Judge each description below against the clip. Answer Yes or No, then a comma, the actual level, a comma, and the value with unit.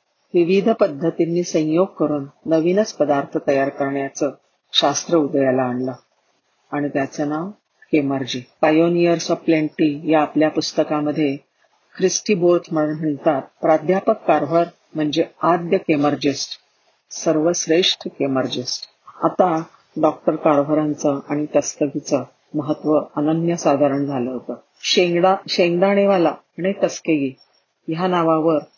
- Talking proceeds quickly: No, average, 85 wpm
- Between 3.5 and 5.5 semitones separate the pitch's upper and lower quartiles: No, average, 2.9 semitones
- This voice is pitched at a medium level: Yes, medium, 155 Hz